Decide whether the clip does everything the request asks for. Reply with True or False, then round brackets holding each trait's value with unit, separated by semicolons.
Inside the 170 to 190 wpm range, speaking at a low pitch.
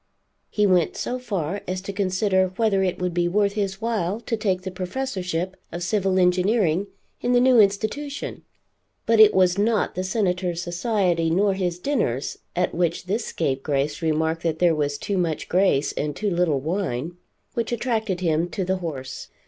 False (175 wpm; 185 Hz)